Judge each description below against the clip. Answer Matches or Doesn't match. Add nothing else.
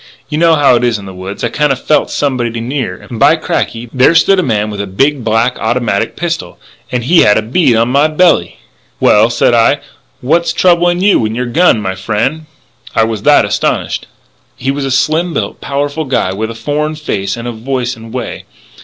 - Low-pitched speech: Matches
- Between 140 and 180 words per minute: Doesn't match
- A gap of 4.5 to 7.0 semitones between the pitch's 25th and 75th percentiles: Matches